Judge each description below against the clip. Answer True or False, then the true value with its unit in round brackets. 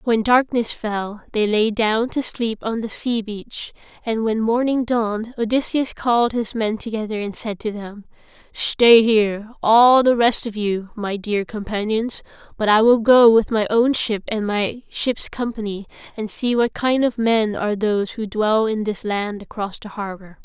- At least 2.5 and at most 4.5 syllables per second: True (4.3 syllables/s)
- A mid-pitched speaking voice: False (220 Hz)